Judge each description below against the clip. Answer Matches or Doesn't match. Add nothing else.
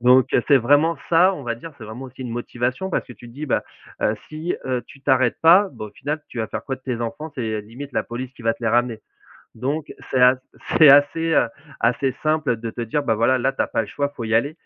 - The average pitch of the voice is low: Matches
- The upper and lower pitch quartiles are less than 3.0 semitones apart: Doesn't match